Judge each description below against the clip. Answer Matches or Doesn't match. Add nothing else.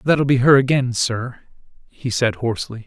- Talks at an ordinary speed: Matches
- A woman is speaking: Doesn't match